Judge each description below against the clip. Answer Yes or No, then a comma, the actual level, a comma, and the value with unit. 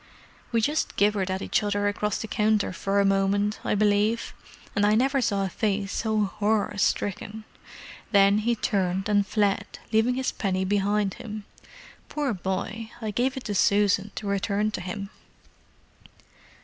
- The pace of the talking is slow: No, average, 150 wpm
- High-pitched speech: Yes, high, 205 Hz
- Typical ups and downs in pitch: No, narrow, 1.6 semitones